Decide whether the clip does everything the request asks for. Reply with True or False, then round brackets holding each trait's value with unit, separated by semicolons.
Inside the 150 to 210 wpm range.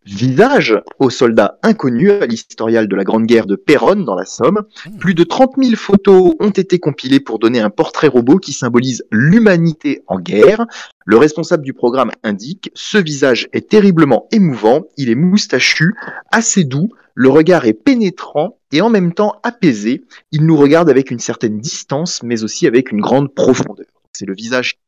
True (175 wpm)